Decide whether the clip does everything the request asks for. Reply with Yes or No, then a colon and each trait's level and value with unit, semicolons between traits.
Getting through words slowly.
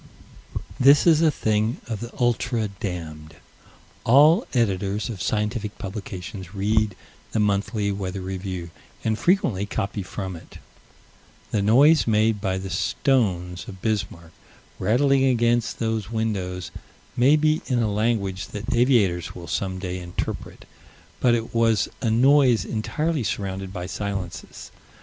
Yes: slow, 130 wpm